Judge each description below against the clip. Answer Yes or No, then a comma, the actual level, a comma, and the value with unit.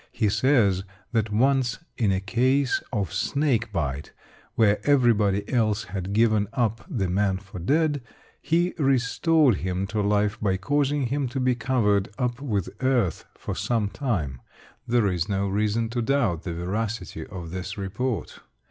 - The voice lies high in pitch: No, low, 110 Hz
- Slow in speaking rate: No, average, 155 wpm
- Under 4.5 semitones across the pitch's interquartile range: No, average, 4.8 semitones